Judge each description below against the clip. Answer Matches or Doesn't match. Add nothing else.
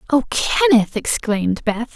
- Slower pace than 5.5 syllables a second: Doesn't match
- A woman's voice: Matches